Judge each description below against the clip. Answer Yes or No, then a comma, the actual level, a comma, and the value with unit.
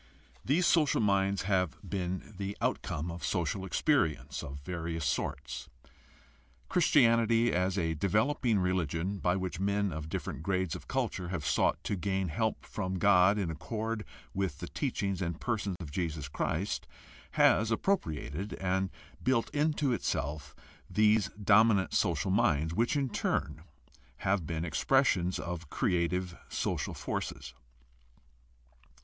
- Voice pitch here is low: Yes, very low, 95 Hz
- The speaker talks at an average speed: No, slow, 130 wpm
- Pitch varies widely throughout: No, average, 4.1 semitones